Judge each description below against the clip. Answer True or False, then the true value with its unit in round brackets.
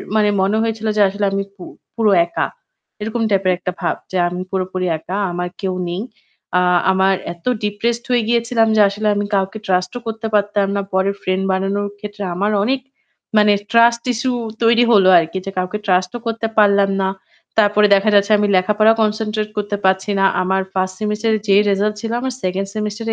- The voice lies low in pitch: False (205 Hz)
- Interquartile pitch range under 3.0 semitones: True (2.4 semitones)